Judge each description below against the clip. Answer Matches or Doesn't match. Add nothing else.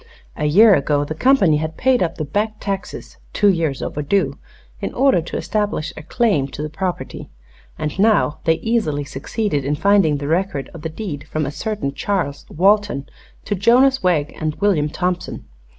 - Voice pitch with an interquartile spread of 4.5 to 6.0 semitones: Matches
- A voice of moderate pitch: Matches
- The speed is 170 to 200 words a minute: Matches